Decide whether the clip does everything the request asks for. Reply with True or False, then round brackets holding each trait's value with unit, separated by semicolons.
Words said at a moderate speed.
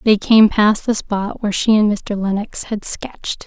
False (210 wpm)